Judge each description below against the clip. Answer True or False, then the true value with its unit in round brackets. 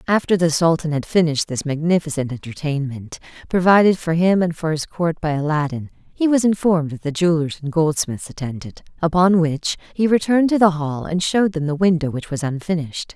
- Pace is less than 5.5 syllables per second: False (5.8 syllables/s)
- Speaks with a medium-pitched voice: True (165 Hz)